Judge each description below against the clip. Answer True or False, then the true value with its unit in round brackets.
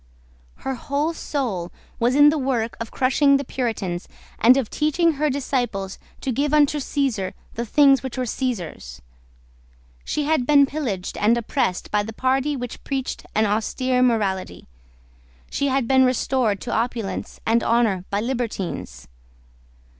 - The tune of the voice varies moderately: True (4.2 semitones)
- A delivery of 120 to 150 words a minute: True (145 wpm)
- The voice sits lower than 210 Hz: False (250 Hz)